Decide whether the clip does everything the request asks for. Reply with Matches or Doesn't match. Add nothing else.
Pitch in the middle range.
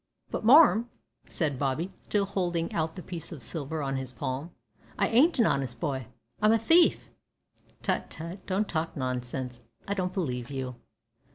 Matches